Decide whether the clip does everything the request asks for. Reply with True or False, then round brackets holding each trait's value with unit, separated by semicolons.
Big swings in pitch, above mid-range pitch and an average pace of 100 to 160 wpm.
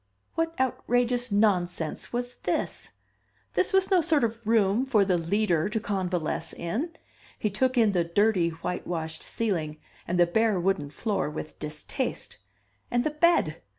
True (6.0 semitones; 205 Hz; 155 wpm)